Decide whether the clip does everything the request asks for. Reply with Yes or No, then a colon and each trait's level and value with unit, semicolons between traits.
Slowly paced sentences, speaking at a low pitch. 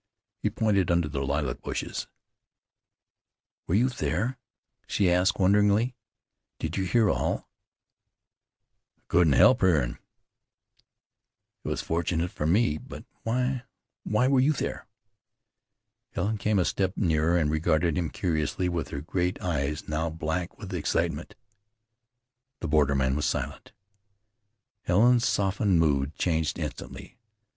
Yes: slow, 125 wpm; very low, 90 Hz